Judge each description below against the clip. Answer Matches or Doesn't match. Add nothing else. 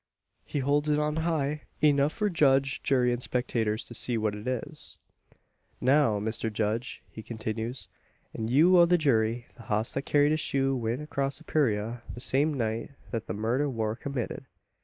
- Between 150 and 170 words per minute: Doesn't match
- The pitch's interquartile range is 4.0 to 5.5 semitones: Matches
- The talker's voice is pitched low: Matches